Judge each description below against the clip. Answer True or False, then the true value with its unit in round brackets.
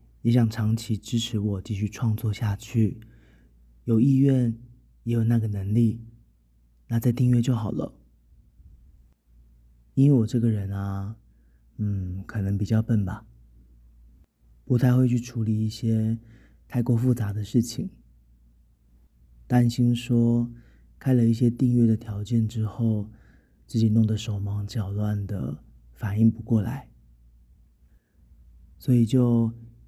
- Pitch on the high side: False (105 Hz)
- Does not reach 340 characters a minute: True (180 characters per minute)